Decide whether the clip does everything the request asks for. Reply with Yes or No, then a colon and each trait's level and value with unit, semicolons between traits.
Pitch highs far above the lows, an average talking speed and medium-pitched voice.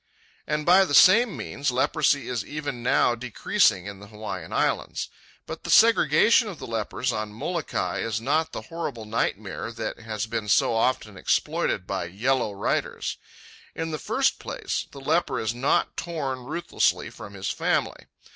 No: wide, 5.9 semitones; average, 160 wpm; low, 125 Hz